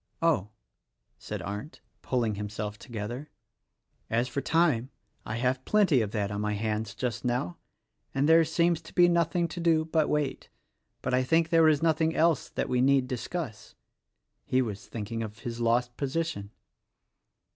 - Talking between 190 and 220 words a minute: No, average, 165 wpm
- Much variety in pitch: Yes, wide, 6.4 semitones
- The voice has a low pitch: Yes, low, 130 Hz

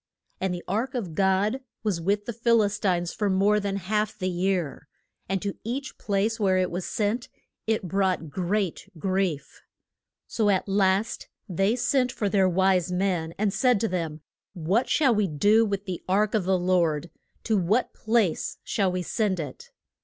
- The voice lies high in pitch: Yes, high, 195 Hz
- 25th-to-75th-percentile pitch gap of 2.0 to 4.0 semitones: Yes, average, 2.8 semitones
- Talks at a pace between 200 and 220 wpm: No, average, 175 wpm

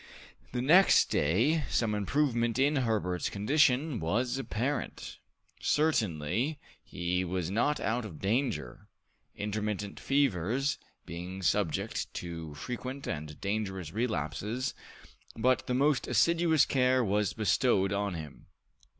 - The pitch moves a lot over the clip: Yes, wide, 6.2 semitones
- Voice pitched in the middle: No, low, 110 Hz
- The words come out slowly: Yes, slow, 110 wpm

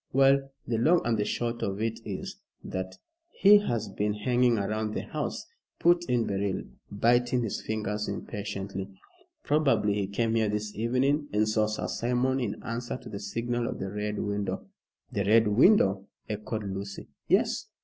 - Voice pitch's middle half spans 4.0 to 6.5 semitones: No, average, 3.1 semitones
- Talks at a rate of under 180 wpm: Yes, average, 165 wpm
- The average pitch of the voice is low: Yes, low, 110 Hz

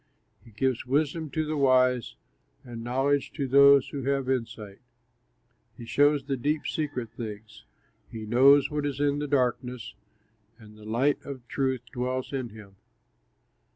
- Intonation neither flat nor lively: Yes, average, 3.2 semitones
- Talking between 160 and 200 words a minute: No, average, 150 wpm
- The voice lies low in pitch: Yes, low, 130 Hz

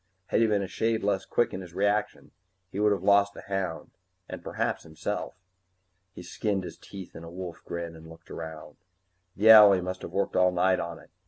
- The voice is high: No, very low, 95 Hz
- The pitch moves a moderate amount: Yes, average, 3.0 semitones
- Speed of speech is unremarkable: No, fast, 210 wpm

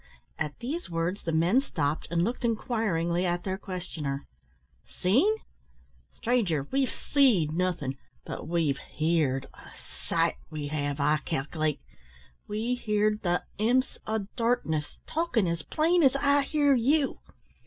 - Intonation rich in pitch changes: Yes, wide, 7.9 semitones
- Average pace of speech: No, slow, 130 wpm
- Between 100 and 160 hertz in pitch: No, medium, 185 Hz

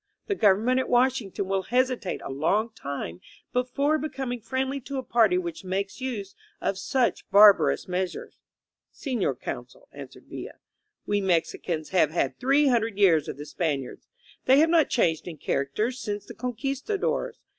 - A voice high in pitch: Yes, high, 220 Hz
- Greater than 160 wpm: No, average, 155 wpm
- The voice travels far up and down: Yes, wide, 6.1 semitones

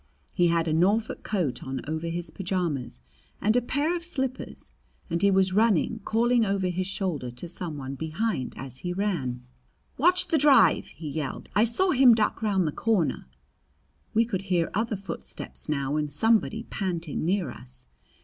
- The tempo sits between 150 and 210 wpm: Yes, average, 170 wpm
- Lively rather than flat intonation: Yes, wide, 6.2 semitones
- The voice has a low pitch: No, medium, 185 Hz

